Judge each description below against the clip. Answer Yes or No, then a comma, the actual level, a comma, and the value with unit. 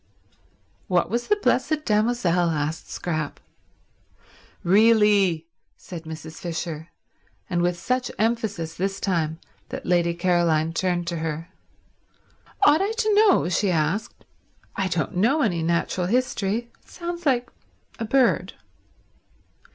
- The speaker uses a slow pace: Yes, slow, 120 wpm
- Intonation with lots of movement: Yes, wide, 5.9 semitones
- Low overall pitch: No, medium, 185 Hz